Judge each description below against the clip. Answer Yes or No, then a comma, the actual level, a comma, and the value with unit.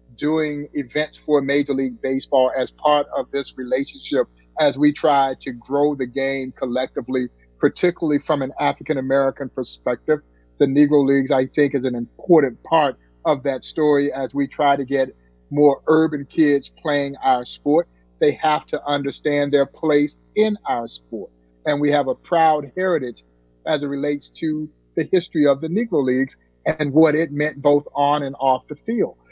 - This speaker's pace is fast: No, average, 170 wpm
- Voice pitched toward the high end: No, medium, 140 Hz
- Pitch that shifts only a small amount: Yes, narrow, 2.3 semitones